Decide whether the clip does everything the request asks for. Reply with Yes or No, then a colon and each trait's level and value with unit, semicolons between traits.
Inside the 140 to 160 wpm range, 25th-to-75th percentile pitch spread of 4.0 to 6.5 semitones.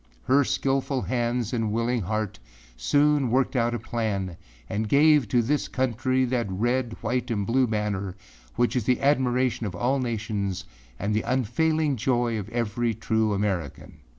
No: average, 155 wpm; average, 3.3 semitones